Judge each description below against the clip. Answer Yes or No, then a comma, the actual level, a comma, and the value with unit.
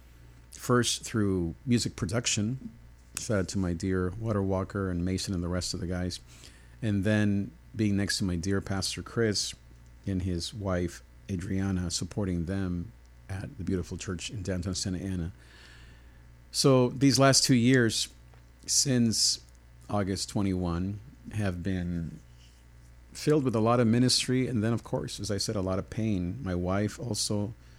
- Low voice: Yes, very low, 95 Hz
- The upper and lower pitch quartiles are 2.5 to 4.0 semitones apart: No, average, 4.9 semitones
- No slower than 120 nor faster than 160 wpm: Yes, average, 150 wpm